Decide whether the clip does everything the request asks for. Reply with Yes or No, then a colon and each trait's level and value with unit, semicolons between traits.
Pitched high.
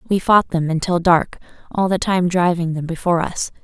No: medium, 175 Hz